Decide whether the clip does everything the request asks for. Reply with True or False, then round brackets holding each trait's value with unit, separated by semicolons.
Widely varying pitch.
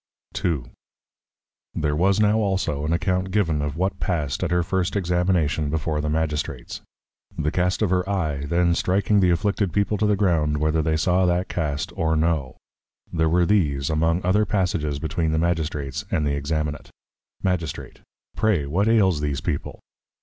False (3.6 semitones)